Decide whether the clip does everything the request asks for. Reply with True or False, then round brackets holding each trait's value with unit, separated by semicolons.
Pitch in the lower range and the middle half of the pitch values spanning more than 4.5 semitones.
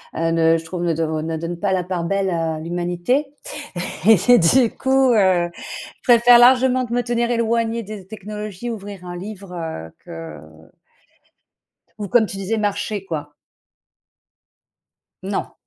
False (195 Hz; 5.5 semitones)